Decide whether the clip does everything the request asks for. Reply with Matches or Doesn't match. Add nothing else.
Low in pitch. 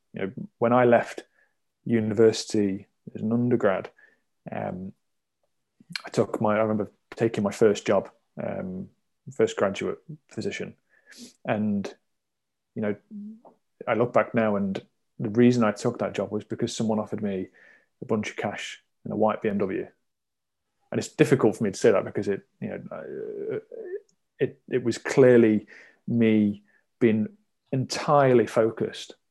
Matches